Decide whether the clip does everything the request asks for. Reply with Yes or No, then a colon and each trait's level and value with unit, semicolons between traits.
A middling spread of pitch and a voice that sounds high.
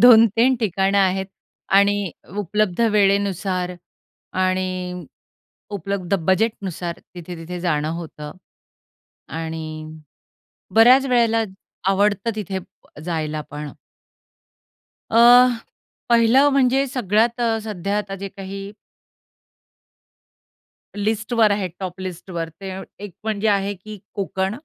Yes: average, 3.3 semitones; high, 200 Hz